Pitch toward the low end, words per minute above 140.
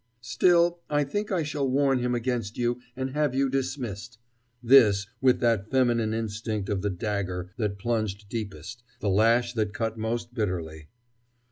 Yes: low, 115 Hz; average, 155 wpm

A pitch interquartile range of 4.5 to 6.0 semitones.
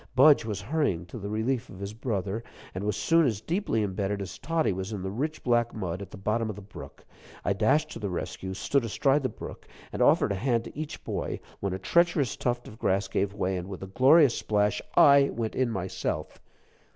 Yes: average, 5.2 semitones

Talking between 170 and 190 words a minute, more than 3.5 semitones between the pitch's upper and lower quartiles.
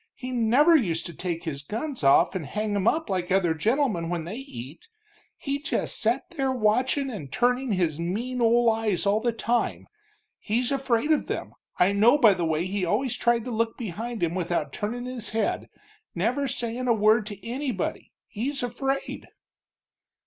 Yes: average, 180 wpm; average, 5.2 semitones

